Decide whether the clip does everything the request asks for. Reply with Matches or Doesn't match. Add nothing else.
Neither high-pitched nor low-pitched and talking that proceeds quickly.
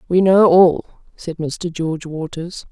Doesn't match